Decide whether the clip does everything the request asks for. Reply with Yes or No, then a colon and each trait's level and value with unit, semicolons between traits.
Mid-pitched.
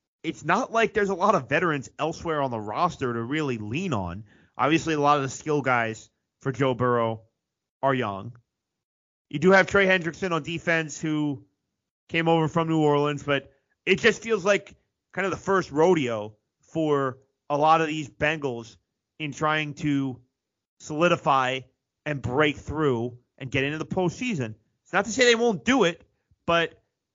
Yes: medium, 150 Hz